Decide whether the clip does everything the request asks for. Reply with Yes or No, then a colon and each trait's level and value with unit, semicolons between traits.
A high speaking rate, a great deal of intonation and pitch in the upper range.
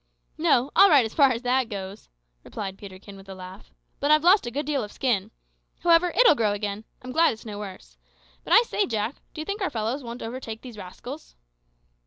Yes: fast, 215 wpm; wide, 6.1 semitones; high, 235 Hz